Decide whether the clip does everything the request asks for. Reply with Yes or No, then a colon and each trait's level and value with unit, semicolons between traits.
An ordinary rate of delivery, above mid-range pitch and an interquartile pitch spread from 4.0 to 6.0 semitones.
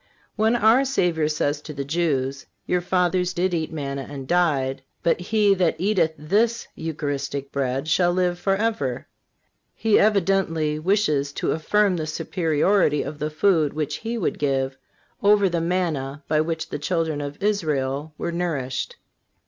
No: average, 150 wpm; medium, 160 Hz; average, 4.5 semitones